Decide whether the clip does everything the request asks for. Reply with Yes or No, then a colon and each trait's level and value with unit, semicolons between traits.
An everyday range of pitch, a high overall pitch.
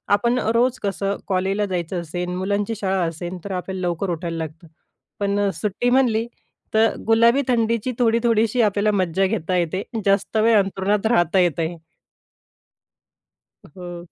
Yes: average, 4.0 semitones; high, 195 Hz